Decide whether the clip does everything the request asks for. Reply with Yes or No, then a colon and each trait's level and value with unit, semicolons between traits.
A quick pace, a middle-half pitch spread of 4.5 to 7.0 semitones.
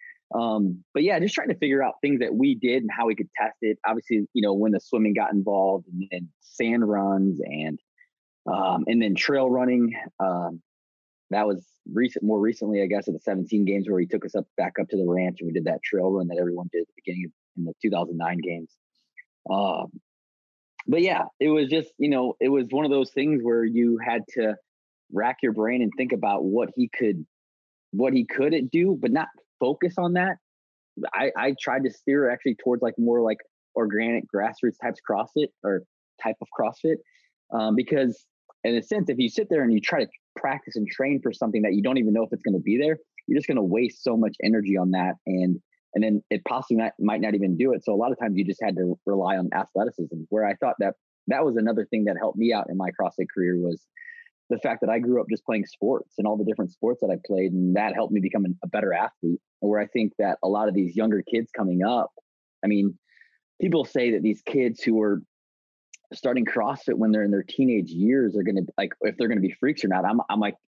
Yes: fast, 235 wpm; average, 4.8 semitones